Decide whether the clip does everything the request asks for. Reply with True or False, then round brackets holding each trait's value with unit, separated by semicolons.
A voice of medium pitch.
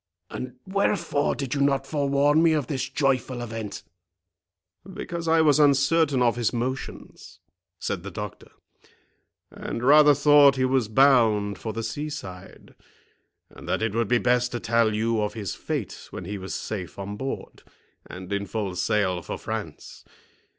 False (120 Hz)